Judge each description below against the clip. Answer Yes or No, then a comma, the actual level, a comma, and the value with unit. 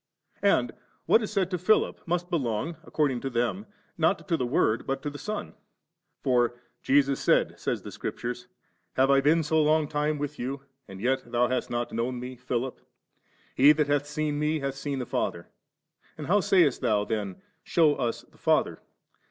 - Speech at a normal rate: Yes, average, 185 wpm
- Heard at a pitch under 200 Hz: Yes, medium, 140 Hz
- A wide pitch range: No, average, 4.2 semitones